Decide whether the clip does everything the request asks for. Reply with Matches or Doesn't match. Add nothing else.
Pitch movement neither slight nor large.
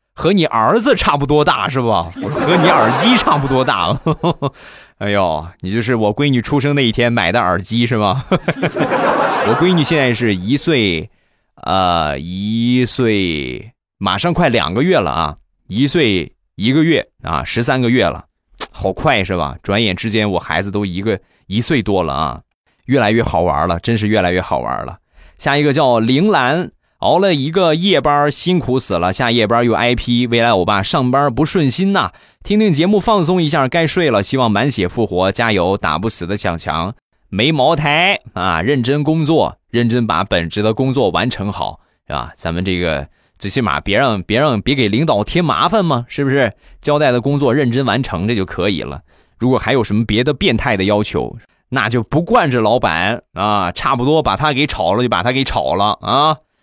Doesn't match